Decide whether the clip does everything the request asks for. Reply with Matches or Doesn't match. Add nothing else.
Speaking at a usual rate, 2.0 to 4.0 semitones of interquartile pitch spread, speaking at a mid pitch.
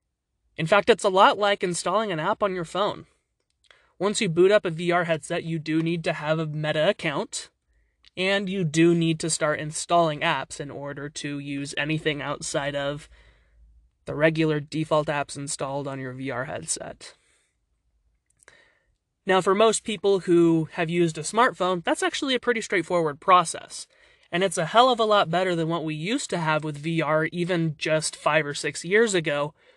Doesn't match